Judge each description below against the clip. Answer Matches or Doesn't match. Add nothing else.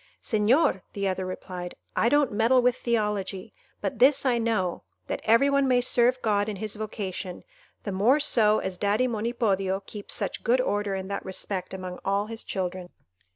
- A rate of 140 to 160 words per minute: Doesn't match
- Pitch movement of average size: Matches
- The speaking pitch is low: Doesn't match